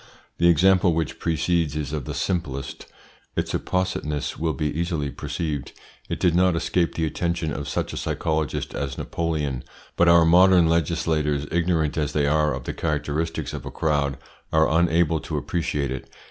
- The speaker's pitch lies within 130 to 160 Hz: No, very low, 80 Hz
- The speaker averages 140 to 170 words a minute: Yes, average, 165 wpm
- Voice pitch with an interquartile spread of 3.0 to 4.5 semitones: No, narrow, 2.5 semitones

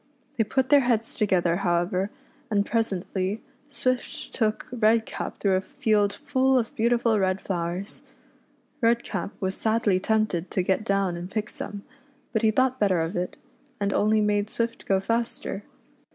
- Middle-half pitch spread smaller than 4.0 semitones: Yes, average, 3.3 semitones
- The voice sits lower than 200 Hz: No, high, 210 Hz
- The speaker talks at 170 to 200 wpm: No, average, 155 wpm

